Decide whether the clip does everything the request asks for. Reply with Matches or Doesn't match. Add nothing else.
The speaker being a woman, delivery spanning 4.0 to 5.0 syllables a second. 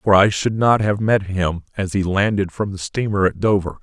Doesn't match